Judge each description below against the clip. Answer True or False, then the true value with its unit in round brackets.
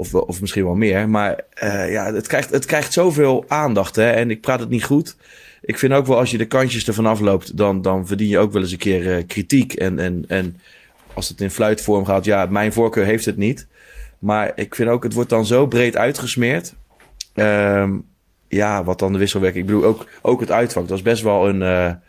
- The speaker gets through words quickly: True (230 wpm)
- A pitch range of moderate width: True (3.4 semitones)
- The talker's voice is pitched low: True (105 Hz)